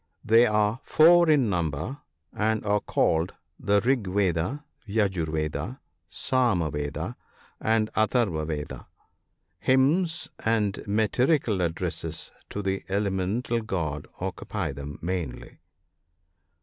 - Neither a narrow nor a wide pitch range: No, wide, 5.9 semitones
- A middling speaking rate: No, slow, 105 wpm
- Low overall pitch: Yes, low, 105 Hz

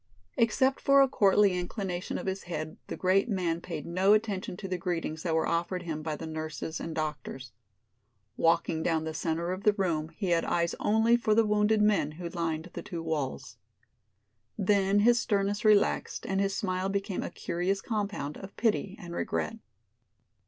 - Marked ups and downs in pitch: No, average, 3.9 semitones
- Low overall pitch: No, medium, 185 Hz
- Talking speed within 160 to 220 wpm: Yes, average, 180 wpm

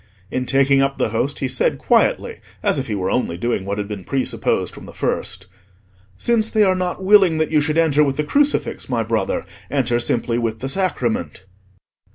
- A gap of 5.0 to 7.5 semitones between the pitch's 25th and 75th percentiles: Yes, wide, 5.6 semitones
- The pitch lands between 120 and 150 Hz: Yes, low, 135 Hz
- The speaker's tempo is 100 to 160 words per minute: No, average, 200 wpm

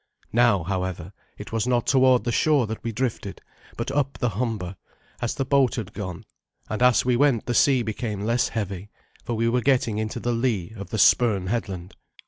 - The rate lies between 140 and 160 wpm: No, average, 195 wpm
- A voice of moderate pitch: No, low, 115 Hz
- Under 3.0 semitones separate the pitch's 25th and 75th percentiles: No, average, 3.6 semitones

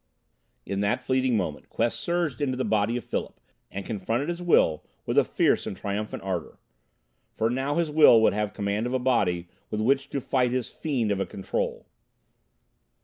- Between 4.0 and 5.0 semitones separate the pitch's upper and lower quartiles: Yes, average, 4.7 semitones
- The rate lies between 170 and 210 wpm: Yes, average, 185 wpm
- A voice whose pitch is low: Yes, low, 115 Hz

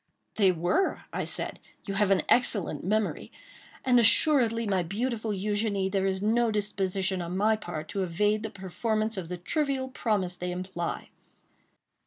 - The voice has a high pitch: Yes, high, 205 Hz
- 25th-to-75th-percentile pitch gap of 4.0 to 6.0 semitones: No, average, 3.1 semitones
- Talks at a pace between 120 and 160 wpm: Yes, average, 155 wpm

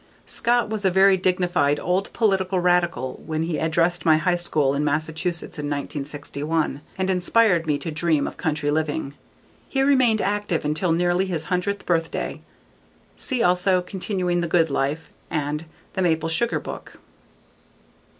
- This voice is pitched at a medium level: Yes, medium, 175 Hz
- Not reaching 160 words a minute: Yes, average, 150 wpm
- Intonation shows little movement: No, average, 3.4 semitones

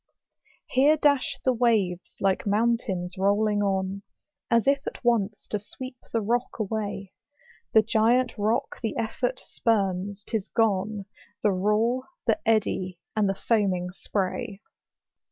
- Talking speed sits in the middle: No, slow, 130 wpm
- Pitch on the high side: Yes, high, 215 Hz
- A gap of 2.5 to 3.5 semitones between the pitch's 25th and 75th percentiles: Yes, average, 3.2 semitones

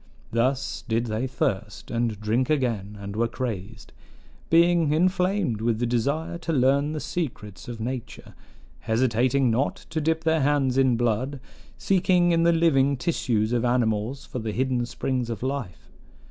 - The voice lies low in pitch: Yes, low, 130 Hz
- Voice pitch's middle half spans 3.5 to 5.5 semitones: Yes, average, 4.8 semitones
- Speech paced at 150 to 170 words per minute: Yes, average, 155 wpm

